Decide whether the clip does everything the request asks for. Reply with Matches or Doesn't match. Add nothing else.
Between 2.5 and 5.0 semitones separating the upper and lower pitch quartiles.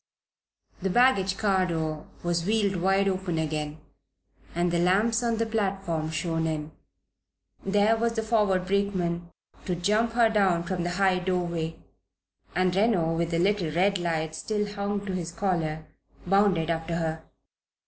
Matches